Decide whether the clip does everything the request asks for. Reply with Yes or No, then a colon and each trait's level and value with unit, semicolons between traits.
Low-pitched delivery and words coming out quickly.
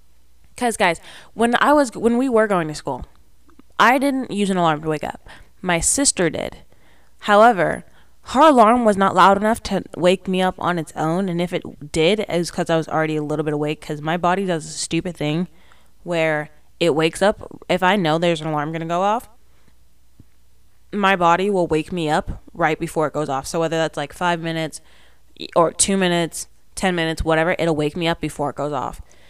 No: medium, 165 Hz; fast, 210 wpm